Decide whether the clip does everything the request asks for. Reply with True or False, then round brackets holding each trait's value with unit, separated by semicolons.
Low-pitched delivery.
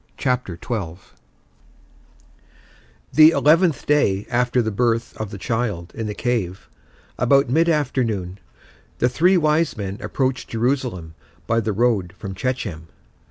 True (120 Hz)